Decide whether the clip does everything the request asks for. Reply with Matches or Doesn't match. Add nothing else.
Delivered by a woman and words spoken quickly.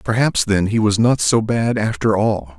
Doesn't match